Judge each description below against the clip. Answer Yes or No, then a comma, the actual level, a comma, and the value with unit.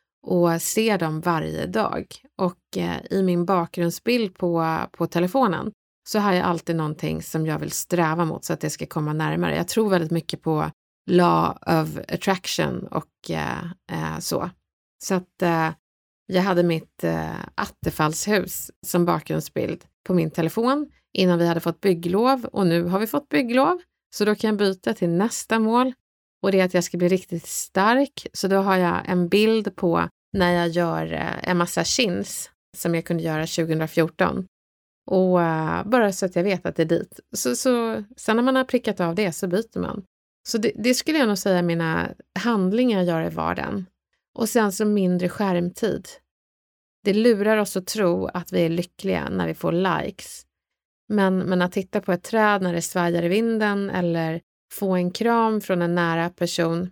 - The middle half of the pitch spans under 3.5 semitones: No, average, 3.8 semitones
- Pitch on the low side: No, medium, 180 Hz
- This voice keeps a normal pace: Yes, average, 180 wpm